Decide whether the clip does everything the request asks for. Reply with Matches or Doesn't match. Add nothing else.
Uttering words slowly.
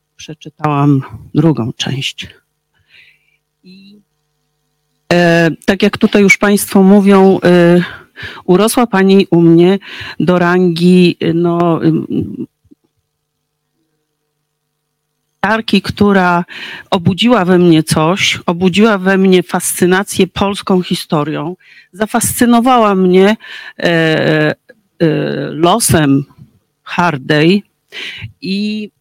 Matches